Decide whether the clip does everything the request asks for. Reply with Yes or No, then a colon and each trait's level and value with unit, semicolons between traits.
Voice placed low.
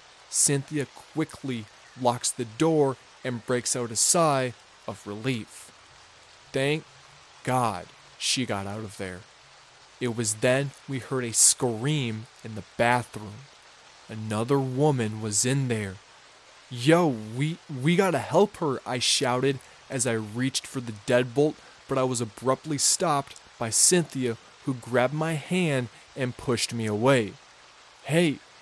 Yes: low, 125 Hz